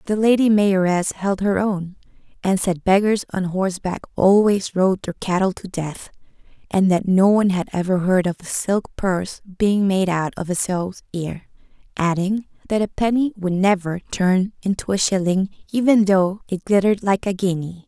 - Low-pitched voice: No, high, 190 Hz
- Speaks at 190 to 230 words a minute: No, average, 175 wpm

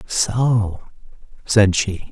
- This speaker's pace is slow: Yes, slow, 85 wpm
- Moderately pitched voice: No, low, 105 Hz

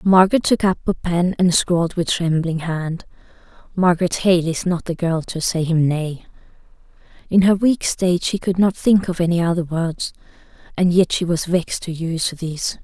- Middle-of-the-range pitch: Yes, medium, 175 Hz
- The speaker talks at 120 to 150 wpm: No, average, 185 wpm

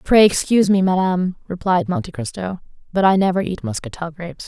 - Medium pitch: Yes, medium, 180 Hz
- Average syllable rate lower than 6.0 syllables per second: No, 6.1 syllables/s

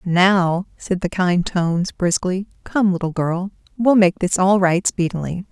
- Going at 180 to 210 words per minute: No, average, 165 wpm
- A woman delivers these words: Yes, female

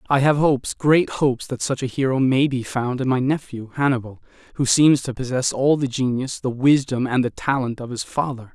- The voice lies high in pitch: No, low, 130 Hz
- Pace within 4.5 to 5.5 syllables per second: Yes, 5.3 syllables/s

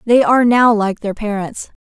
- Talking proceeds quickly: No, average, 195 wpm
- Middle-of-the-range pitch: No, high, 220 Hz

